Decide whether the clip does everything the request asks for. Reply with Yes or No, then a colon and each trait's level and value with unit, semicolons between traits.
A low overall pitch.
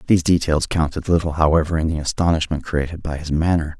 Yes: very low, 80 Hz